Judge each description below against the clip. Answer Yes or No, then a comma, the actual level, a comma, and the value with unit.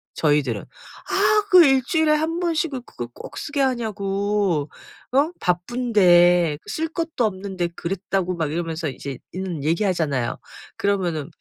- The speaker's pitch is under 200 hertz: Yes, high, 190 Hz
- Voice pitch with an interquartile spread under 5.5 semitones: No, wide, 7.9 semitones